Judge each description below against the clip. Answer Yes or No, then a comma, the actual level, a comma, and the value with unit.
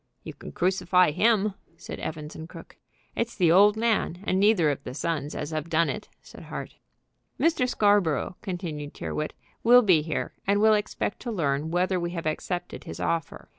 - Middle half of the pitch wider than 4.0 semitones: Yes, average, 4.8 semitones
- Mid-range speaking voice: Yes, medium, 180 Hz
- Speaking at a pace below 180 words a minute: No, average, 185 wpm